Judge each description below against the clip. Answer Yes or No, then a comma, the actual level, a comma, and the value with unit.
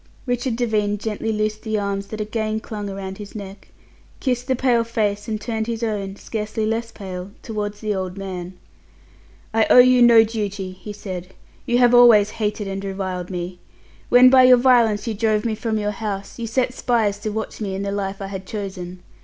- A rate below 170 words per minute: No, average, 195 wpm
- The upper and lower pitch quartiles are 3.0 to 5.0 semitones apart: No, narrow, 2.5 semitones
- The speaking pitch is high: Yes, high, 210 Hz